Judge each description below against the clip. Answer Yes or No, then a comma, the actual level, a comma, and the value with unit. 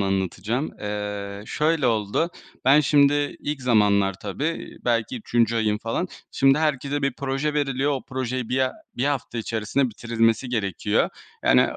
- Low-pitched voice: Yes, low, 125 Hz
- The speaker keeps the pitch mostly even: No, average, 4.8 semitones